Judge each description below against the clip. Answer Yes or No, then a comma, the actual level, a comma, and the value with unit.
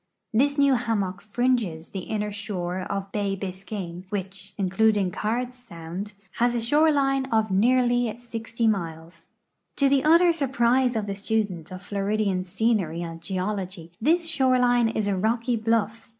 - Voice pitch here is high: Yes, high, 215 Hz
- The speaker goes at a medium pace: Yes, average, 150 wpm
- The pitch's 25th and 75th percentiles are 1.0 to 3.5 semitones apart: No, average, 4.3 semitones